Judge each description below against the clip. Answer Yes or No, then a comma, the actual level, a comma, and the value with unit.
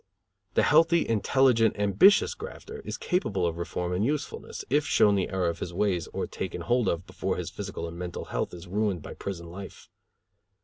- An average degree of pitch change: No, wide, 6.3 semitones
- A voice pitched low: Yes, low, 100 Hz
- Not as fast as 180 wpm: No, average, 185 wpm